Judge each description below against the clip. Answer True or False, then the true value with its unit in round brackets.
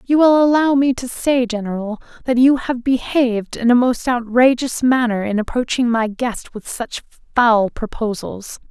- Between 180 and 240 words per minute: False (165 wpm)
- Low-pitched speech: False (240 Hz)